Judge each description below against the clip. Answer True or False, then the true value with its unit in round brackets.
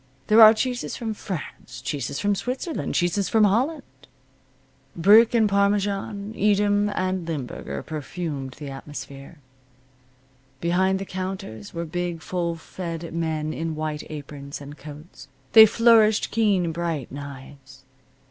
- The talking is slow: True (125 wpm)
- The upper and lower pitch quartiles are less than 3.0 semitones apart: False (5.5 semitones)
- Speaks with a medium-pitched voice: True (175 Hz)